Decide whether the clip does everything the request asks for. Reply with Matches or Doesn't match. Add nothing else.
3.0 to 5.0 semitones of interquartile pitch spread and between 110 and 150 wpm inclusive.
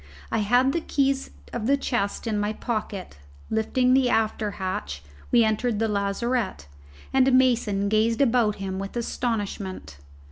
Matches